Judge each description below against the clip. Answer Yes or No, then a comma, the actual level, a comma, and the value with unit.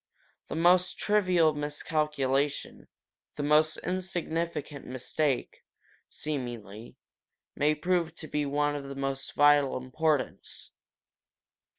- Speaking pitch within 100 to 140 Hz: No, medium, 150 Hz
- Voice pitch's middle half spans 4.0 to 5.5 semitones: No, average, 2.7 semitones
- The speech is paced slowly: Yes, slow, 90 wpm